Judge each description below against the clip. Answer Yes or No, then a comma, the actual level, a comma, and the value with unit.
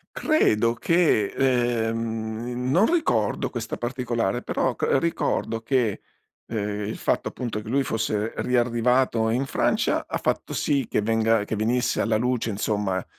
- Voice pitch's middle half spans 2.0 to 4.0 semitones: Yes, narrow, 2.4 semitones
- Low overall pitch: Yes, low, 115 Hz